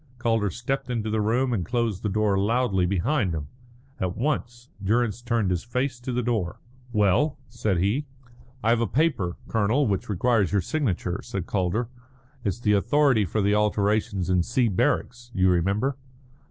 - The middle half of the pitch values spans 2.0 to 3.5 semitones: No, average, 4.0 semitones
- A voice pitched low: Yes, low, 110 Hz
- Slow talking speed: No, average, 165 wpm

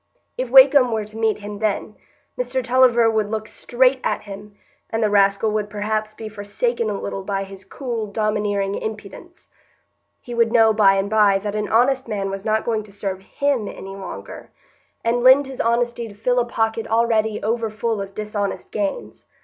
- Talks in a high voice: Yes, high, 215 Hz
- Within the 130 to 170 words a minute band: No, average, 185 wpm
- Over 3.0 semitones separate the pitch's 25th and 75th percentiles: No, narrow, 2.5 semitones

